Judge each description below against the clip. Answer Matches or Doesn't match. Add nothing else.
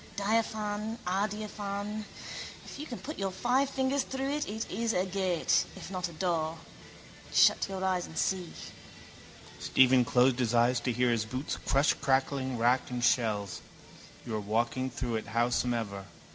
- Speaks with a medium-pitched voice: Matches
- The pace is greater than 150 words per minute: Matches